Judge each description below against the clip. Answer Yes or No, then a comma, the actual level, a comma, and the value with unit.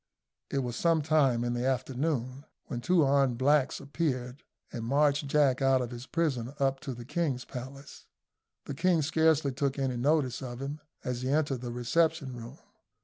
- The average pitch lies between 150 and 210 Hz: No, low, 135 Hz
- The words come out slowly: No, average, 170 wpm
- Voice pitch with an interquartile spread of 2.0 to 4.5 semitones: Yes, average, 3.0 semitones